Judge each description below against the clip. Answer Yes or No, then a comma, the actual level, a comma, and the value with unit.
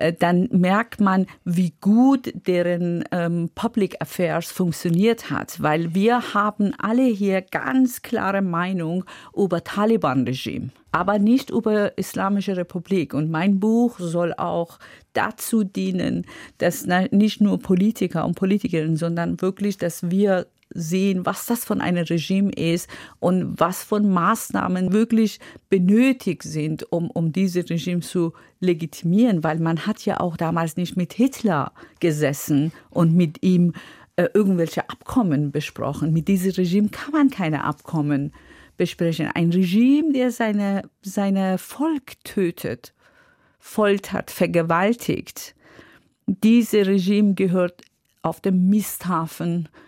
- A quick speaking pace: No, slow, 125 wpm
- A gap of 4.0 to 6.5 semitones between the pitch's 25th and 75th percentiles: No, average, 3.5 semitones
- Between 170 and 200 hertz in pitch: Yes, medium, 185 Hz